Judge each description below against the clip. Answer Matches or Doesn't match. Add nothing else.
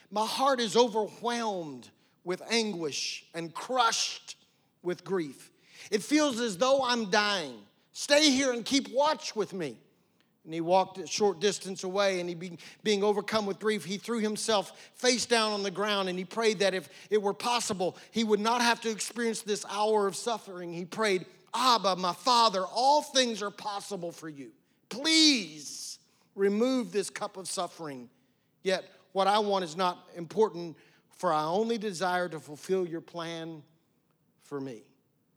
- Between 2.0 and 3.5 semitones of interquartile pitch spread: Doesn't match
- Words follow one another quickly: Doesn't match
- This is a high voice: Matches